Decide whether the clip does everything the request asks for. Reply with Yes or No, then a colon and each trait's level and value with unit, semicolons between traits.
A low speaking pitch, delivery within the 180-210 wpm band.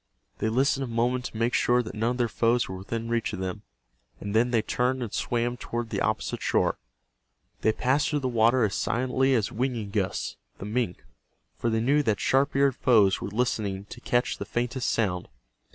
Yes: low, 120 Hz; average, 200 wpm